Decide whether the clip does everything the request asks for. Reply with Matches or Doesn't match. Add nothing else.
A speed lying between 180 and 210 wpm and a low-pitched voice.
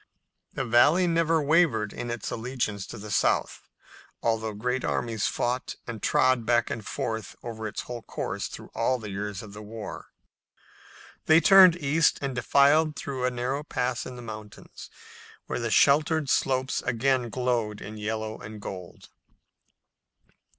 Doesn't match